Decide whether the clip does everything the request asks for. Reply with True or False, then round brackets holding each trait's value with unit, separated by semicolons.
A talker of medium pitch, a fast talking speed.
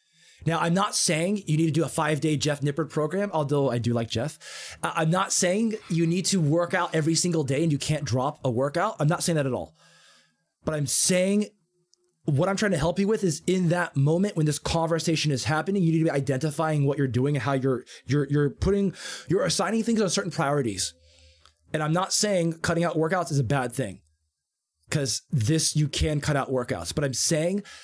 True (155 Hz; 220 wpm)